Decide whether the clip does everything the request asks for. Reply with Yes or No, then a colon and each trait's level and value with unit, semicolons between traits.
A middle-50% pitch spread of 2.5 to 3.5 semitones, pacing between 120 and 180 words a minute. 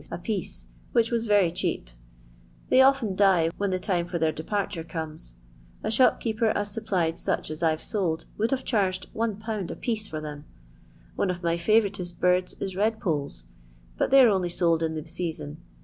No: average, 4.6 semitones; average, 165 wpm